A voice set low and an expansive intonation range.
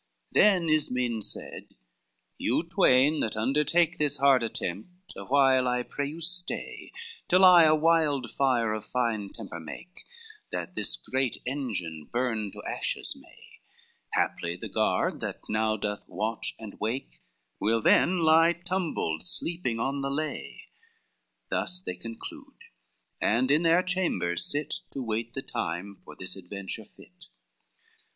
Yes: low, 130 Hz; wide, 6.5 semitones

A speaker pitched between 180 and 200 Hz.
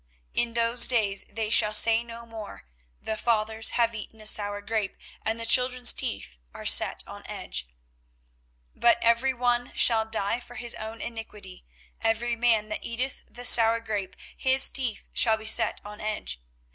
No: high, 225 Hz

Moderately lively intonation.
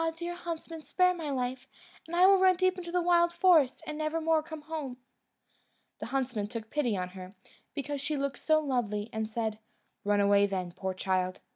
No: wide, 7.4 semitones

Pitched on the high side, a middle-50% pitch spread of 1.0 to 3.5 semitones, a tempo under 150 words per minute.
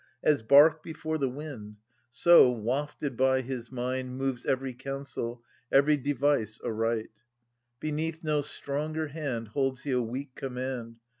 No: low, 135 Hz; average, 3.1 semitones; slow, 135 wpm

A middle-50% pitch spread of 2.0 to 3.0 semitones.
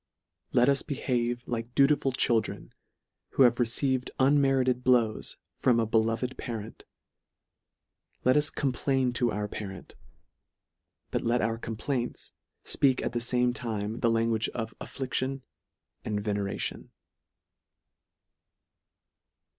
Yes: narrow, 2.5 semitones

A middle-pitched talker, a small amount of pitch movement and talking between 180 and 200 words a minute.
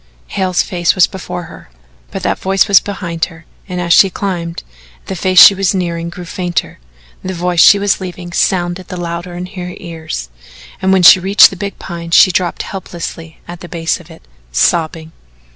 Yes: medium, 180 Hz; narrow, 1.8 semitones; average, 190 wpm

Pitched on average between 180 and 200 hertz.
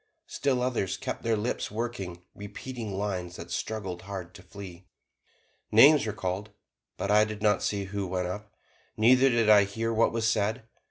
No: low, 105 Hz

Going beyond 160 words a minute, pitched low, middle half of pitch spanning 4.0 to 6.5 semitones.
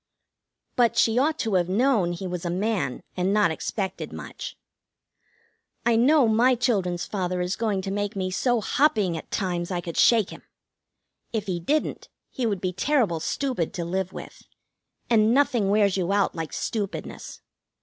No: average, 170 wpm; high, 200 Hz; average, 4.4 semitones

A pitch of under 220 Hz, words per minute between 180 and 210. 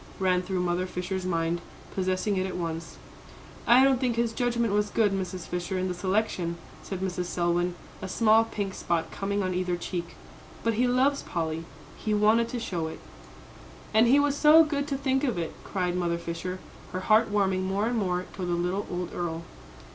Yes: high, 190 Hz; average, 195 wpm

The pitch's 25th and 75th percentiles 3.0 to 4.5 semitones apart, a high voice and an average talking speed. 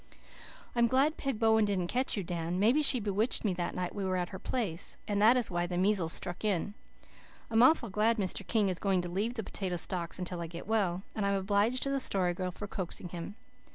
No: average, 3.8 semitones; high, 200 Hz; fast, 230 wpm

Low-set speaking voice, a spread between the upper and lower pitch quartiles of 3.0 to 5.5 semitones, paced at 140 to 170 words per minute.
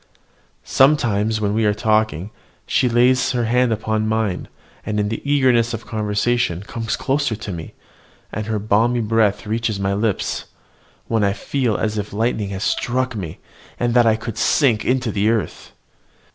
No: low, 110 Hz; narrow, 2.4 semitones; average, 165 wpm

